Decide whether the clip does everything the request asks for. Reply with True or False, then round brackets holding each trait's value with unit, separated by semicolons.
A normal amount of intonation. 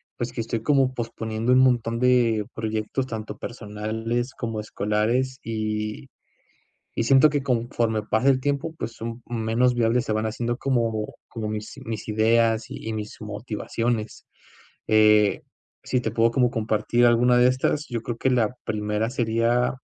False (2.2 semitones)